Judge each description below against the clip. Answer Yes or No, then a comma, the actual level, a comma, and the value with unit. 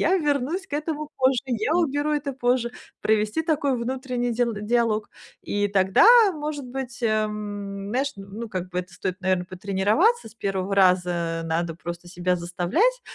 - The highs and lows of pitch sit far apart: Yes, wide, 6.7 semitones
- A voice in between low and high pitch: No, high, 225 Hz